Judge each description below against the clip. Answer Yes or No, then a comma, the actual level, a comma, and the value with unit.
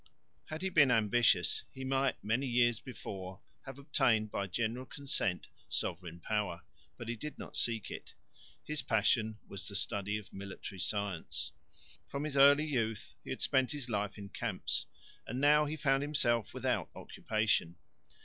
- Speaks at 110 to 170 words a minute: Yes, average, 160 wpm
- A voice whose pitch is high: No, low, 115 Hz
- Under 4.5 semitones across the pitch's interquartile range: No, average, 5.1 semitones